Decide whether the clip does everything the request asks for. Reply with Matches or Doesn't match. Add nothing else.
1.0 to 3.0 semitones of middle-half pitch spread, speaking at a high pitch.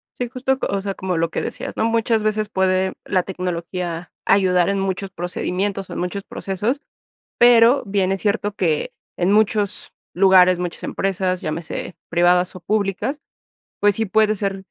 Matches